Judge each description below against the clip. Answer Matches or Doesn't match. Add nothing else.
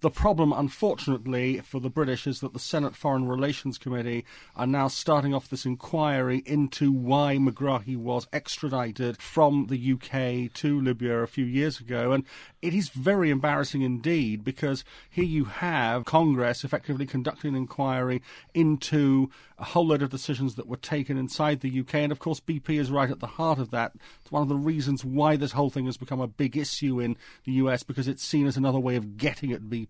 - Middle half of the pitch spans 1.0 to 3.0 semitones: Matches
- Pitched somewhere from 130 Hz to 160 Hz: Matches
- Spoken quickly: Doesn't match